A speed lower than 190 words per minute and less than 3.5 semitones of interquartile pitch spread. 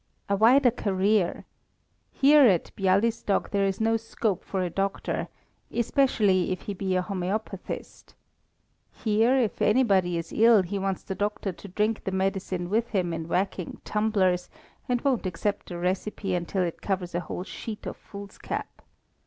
Yes: average, 155 wpm; average, 2.9 semitones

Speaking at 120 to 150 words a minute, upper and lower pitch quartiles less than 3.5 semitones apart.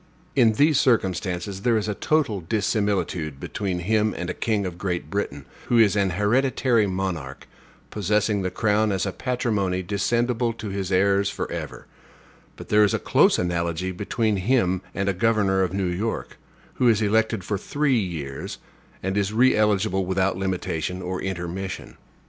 No: average, 160 wpm; average, 3.0 semitones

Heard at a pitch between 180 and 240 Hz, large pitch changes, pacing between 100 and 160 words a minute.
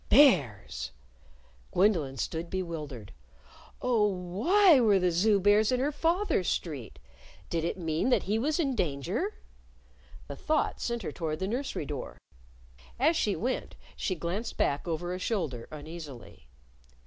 Yes: medium, 185 Hz; wide, 7.3 semitones; average, 140 wpm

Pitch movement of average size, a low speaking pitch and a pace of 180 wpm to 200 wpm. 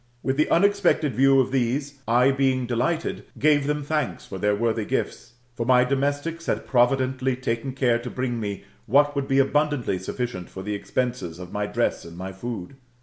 Yes: average, 3.2 semitones; low, 130 Hz; average, 185 wpm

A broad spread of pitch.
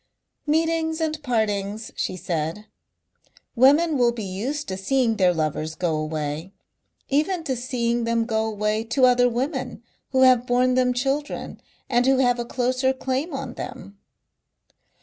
No: average, 4.0 semitones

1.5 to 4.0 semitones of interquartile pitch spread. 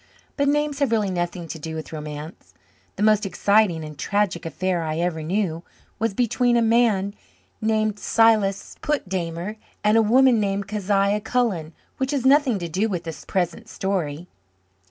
No: average, 4.6 semitones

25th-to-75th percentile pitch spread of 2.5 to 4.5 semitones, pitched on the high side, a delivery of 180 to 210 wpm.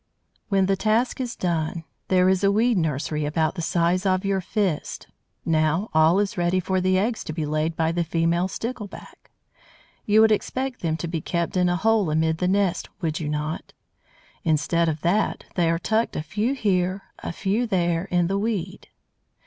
No: average, 3.5 semitones; medium, 180 Hz; average, 190 wpm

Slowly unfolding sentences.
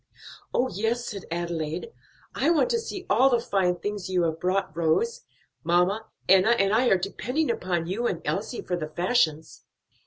No: average, 175 wpm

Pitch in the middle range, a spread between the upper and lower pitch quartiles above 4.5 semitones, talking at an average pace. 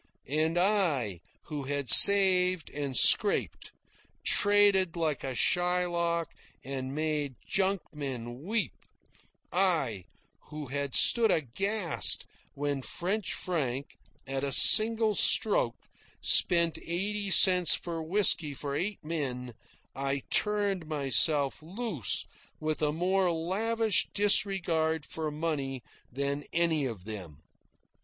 No: medium, 160 Hz; average, 5.2 semitones; slow, 105 wpm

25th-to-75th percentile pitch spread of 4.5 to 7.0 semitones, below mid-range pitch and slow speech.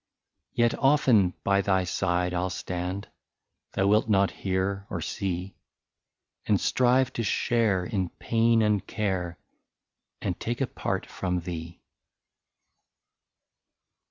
No: average, 3.9 semitones; low, 100 Hz; slow, 130 wpm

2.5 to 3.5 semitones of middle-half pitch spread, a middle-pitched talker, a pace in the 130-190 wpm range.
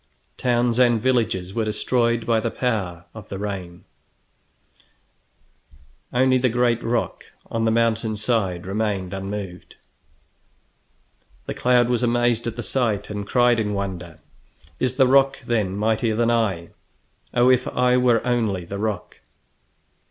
No: average, 3.2 semitones; low, 115 Hz; slow, 135 wpm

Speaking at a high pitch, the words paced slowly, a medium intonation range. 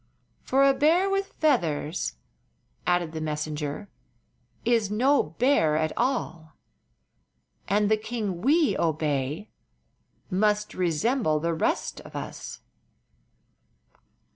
No: high, 195 Hz; slow, 100 wpm; wide, 7.9 semitones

